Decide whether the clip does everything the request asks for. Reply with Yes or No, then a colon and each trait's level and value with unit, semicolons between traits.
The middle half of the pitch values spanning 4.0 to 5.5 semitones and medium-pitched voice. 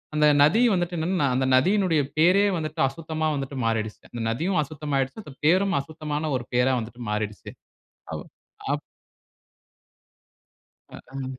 Yes: average, 4.3 semitones; medium, 150 Hz